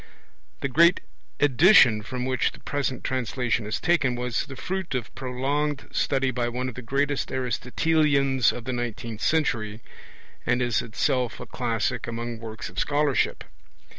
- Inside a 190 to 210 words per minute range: No, average, 150 wpm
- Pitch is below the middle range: Yes, low, 125 Hz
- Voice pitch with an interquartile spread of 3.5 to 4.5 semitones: No, average, 3.1 semitones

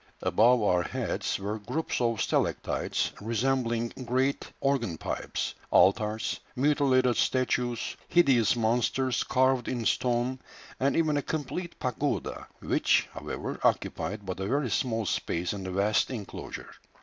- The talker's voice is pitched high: No, low, 120 Hz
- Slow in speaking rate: Yes, slow, 125 wpm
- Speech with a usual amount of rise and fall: Yes, average, 3.6 semitones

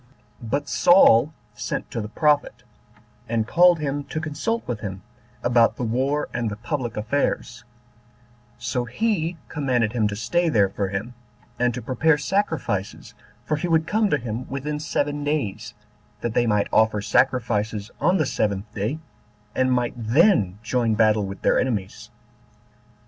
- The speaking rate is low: No, average, 155 wpm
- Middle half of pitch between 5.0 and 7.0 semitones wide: Yes, wide, 5.5 semitones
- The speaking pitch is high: No, low, 125 Hz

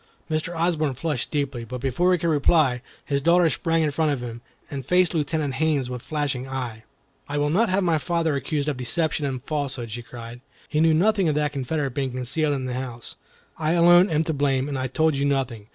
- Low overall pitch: No, medium, 145 Hz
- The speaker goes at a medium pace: No, fast, 215 wpm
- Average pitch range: Yes, average, 3.7 semitones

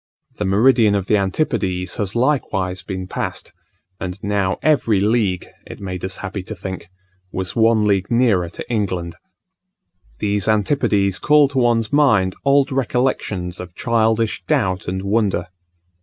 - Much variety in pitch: No, average, 3.7 semitones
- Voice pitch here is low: Yes, low, 100 Hz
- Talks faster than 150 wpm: No, average, 140 wpm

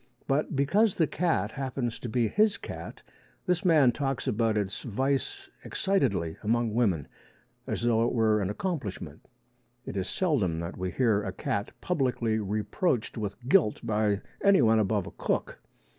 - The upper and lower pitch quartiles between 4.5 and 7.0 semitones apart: Yes, average, 5.2 semitones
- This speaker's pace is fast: No, average, 155 wpm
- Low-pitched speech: Yes, low, 115 Hz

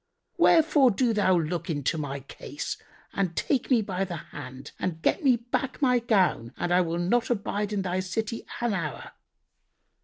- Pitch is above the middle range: Yes, high, 195 Hz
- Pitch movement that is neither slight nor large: No, wide, 5.7 semitones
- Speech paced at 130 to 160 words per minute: No, average, 175 wpm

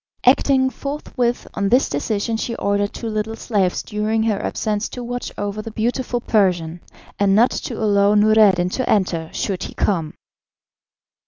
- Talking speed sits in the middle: Yes, average, 155 wpm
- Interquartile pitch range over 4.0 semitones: No, average, 2.9 semitones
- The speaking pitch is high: Yes, high, 215 Hz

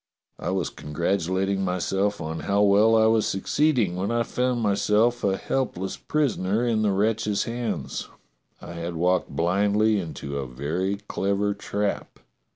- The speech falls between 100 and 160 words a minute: Yes, average, 150 wpm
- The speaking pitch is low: Yes, low, 100 Hz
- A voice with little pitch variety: No, average, 3.3 semitones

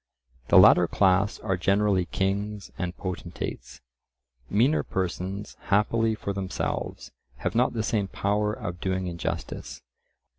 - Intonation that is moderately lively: No, narrow, 2.2 semitones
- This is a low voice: Yes, low, 100 Hz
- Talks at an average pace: No, slow, 120 wpm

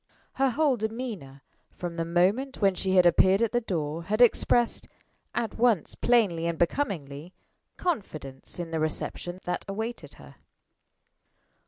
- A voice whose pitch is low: No, high, 190 Hz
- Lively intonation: Yes, wide, 6.0 semitones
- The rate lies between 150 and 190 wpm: No, average, 140 wpm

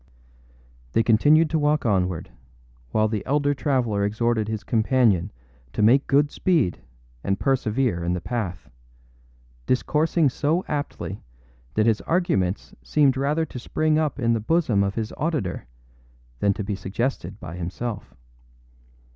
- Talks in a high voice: No, low, 120 Hz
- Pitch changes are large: Yes, wide, 6.1 semitones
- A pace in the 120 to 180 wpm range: Yes, average, 140 wpm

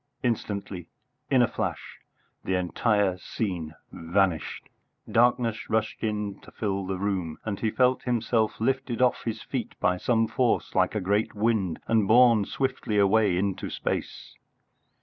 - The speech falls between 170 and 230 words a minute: No, average, 145 wpm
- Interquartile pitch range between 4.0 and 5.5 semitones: No, average, 3.3 semitones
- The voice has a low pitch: Yes, low, 105 Hz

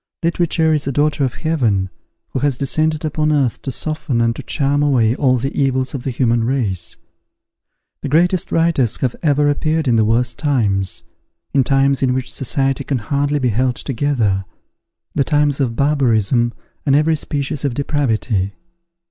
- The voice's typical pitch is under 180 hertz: Yes, low, 135 Hz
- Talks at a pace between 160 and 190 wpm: Yes, average, 165 wpm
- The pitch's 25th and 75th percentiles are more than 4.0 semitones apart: No, average, 3.6 semitones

